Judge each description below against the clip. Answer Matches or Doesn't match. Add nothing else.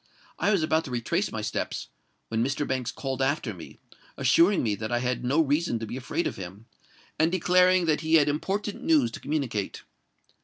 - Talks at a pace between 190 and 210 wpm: Matches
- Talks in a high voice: Doesn't match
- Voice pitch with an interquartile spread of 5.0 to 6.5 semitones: Matches